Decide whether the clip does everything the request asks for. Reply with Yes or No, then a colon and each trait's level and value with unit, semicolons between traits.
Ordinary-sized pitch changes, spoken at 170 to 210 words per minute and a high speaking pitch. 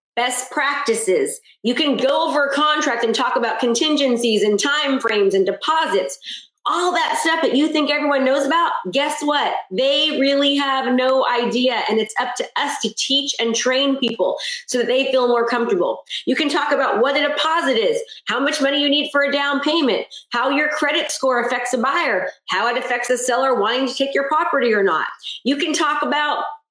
Yes: average, 3.3 semitones; average, 200 wpm; very high, 280 Hz